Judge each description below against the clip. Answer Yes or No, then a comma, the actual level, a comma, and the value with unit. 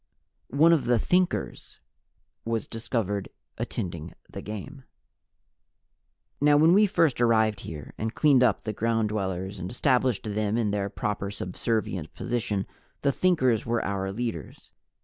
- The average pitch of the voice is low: Yes, low, 110 Hz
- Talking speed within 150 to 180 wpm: No, average, 140 wpm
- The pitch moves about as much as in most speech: Yes, average, 4.2 semitones